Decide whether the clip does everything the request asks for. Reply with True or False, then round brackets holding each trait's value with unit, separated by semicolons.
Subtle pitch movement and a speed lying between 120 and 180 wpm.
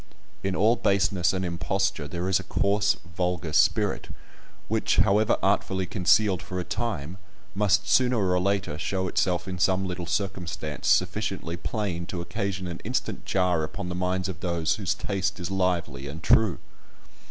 True (2.2 semitones; 160 wpm)